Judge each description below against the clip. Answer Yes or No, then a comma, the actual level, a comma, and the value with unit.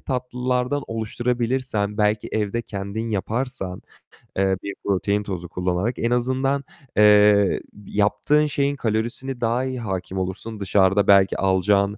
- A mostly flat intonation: No, average, 3.9 semitones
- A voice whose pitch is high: No, low, 105 Hz